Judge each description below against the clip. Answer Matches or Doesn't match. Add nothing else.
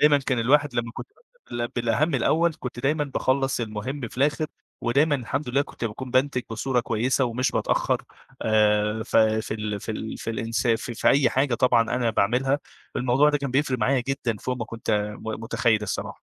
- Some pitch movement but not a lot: Matches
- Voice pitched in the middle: Doesn't match